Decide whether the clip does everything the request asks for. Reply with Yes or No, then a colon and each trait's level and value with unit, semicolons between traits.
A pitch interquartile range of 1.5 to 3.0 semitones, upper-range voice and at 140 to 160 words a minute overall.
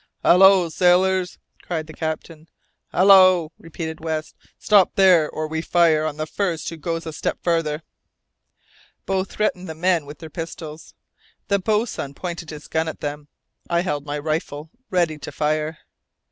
No: average, 2.7 semitones; medium, 165 Hz; average, 155 wpm